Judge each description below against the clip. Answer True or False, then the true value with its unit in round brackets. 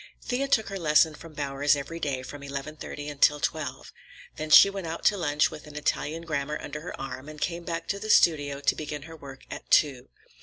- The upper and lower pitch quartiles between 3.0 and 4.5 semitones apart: False (2.6 semitones)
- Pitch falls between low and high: True (150 Hz)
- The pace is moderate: False (220 wpm)